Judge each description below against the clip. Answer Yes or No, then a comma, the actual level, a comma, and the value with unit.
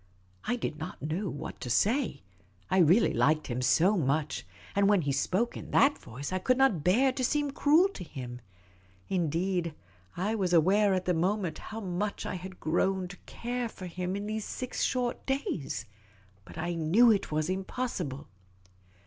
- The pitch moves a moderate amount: No, wide, 5.7 semitones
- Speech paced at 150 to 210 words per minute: Yes, average, 175 wpm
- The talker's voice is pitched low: No, medium, 185 Hz